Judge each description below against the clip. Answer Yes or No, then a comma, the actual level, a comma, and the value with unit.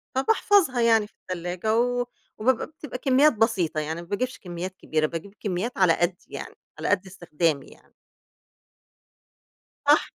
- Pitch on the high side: Yes, high, 200 Hz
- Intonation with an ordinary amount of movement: No, wide, 6.1 semitones